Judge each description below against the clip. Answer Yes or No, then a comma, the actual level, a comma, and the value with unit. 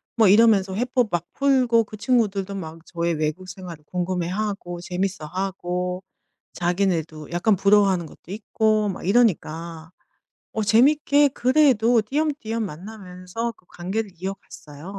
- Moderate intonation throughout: Yes, average, 4.0 semitones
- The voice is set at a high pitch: Yes, high, 195 Hz